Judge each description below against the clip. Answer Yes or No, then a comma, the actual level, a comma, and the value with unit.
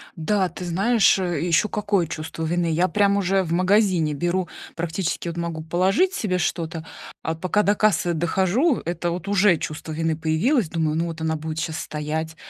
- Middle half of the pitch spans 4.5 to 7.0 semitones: No, average, 3.3 semitones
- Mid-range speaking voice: Yes, medium, 175 Hz